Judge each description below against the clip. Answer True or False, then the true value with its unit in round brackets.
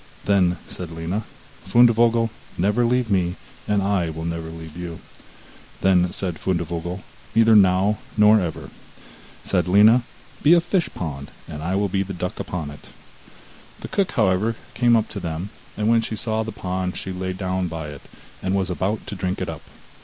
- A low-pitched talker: True (95 Hz)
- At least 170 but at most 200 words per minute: True (175 wpm)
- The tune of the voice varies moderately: True (3.8 semitones)